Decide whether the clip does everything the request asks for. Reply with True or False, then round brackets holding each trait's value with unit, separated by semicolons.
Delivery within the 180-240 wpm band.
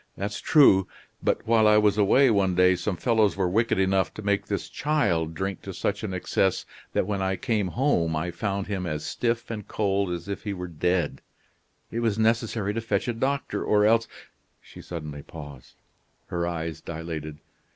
True (190 wpm)